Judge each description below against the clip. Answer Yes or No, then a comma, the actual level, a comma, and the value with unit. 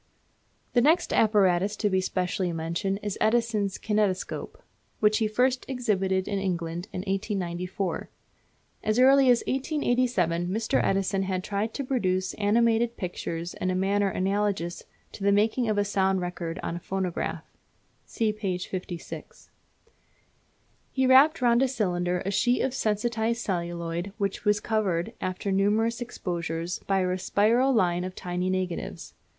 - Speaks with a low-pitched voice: No, high, 195 Hz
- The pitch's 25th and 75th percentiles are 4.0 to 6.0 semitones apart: No, average, 3.6 semitones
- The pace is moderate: Yes, average, 145 wpm